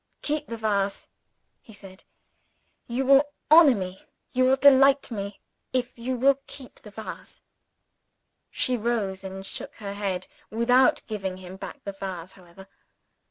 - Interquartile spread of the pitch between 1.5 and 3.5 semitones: No, average, 5.1 semitones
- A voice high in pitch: Yes, high, 220 Hz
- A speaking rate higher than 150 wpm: No, average, 145 wpm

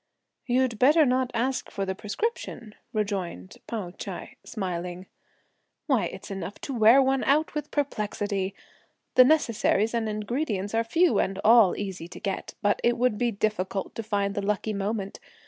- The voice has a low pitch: No, high, 215 Hz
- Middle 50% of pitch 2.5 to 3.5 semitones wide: No, average, 4.1 semitones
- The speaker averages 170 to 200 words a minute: No, average, 160 wpm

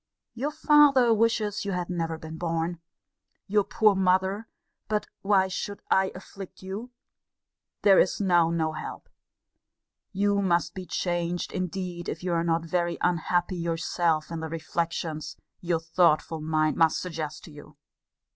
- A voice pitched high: No, medium, 175 Hz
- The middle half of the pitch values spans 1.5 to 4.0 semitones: Yes, average, 3.0 semitones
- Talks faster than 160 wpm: No, average, 145 wpm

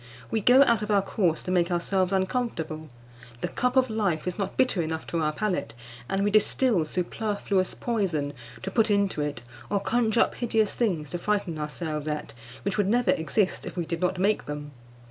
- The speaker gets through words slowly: No, average, 195 wpm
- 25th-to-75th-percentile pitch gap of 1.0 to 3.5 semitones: No, average, 4.9 semitones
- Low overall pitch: No, high, 190 Hz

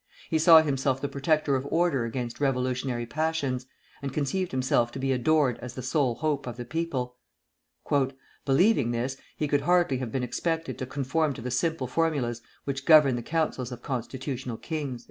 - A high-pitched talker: No, low, 135 Hz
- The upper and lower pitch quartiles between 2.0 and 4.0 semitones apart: Yes, average, 3.7 semitones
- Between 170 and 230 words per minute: Yes, average, 175 wpm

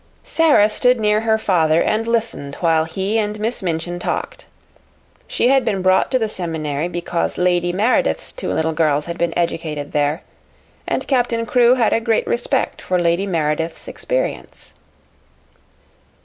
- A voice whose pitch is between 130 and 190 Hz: Yes, medium, 185 Hz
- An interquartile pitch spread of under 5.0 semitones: No, wide, 5.6 semitones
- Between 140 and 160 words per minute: Yes, average, 150 wpm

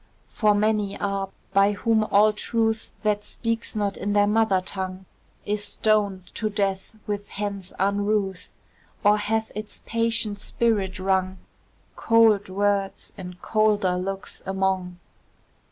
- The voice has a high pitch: Yes, high, 205 Hz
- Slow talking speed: Yes, slow, 125 wpm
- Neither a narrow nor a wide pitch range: No, narrow, 1.8 semitones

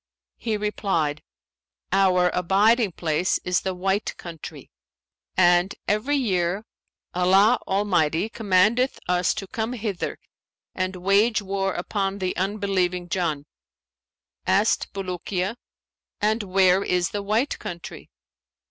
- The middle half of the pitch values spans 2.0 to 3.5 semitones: Yes, narrow, 2.6 semitones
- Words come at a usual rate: No, slow, 110 wpm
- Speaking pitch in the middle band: No, high, 195 Hz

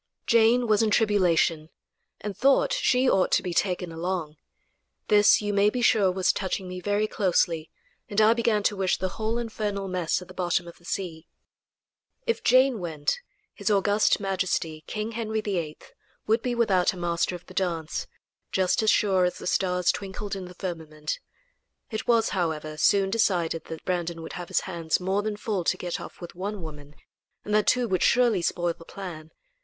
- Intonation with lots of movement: No, average, 3.6 semitones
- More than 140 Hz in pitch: Yes, high, 190 Hz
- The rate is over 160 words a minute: Yes, average, 185 wpm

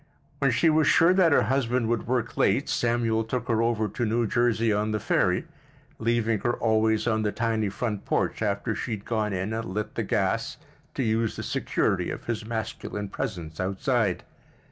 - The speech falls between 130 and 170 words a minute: No, average, 190 wpm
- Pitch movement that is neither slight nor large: No, narrow, 2.0 semitones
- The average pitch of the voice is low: Yes, low, 115 Hz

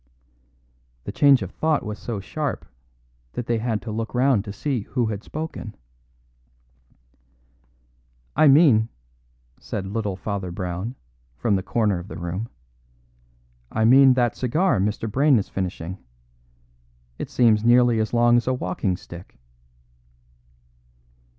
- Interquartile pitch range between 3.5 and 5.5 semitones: Yes, average, 4.1 semitones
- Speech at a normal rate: No, slow, 130 wpm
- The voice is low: Yes, low, 110 Hz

